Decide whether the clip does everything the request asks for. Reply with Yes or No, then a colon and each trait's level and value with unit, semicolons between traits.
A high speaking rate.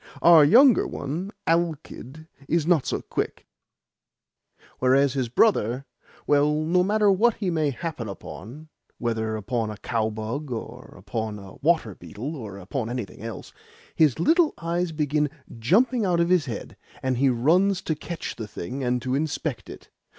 No: average, 155 wpm